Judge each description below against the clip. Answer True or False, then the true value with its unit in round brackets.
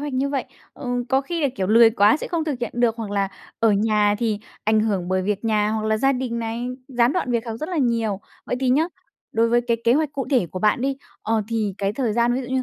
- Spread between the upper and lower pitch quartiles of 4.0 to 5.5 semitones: False (3.3 semitones)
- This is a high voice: True (230 Hz)